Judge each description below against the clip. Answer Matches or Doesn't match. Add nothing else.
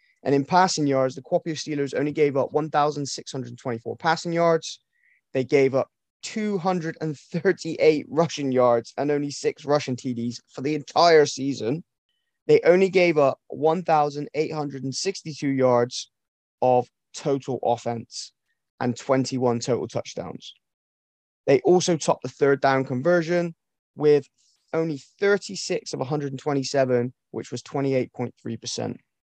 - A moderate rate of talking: Doesn't match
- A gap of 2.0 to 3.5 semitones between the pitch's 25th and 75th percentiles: Doesn't match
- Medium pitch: Matches